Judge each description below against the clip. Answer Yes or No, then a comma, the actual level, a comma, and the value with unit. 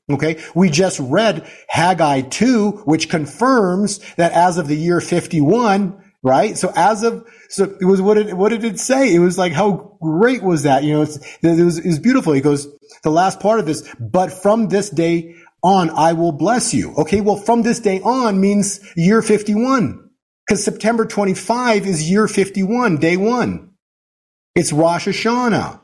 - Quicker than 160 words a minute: Yes, average, 180 wpm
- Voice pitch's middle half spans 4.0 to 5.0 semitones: Yes, average, 4.4 semitones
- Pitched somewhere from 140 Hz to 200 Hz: Yes, high, 190 Hz